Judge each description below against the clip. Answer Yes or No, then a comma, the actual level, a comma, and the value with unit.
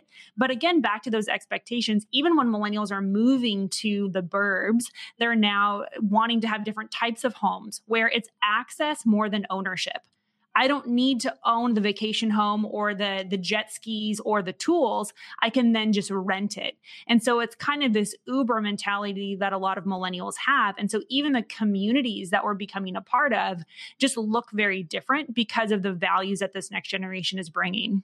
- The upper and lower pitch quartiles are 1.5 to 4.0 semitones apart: Yes, average, 2.9 semitones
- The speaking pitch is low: No, high, 215 Hz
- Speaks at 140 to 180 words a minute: No, average, 195 wpm